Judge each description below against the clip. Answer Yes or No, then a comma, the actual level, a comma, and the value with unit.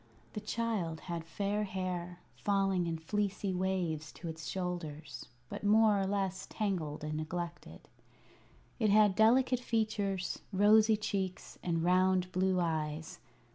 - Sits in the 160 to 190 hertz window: Yes, medium, 185 Hz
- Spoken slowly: Yes, slow, 130 wpm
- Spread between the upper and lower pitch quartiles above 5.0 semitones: No, average, 3.6 semitones